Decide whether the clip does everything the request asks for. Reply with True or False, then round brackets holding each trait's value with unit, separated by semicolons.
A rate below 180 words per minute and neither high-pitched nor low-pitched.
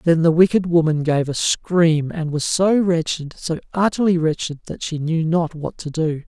False (200 wpm; 165 Hz)